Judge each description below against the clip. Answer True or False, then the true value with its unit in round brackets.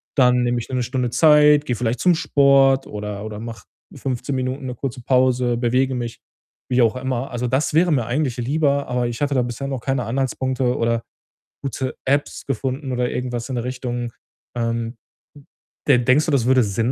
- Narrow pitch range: True (2.1 semitones)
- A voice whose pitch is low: True (125 Hz)